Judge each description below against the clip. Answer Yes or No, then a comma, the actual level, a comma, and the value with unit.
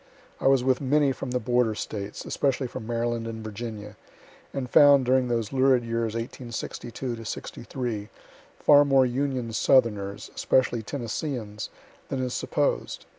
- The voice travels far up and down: No, narrow, 2.6 semitones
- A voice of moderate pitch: No, low, 120 Hz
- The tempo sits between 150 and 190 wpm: No, slow, 135 wpm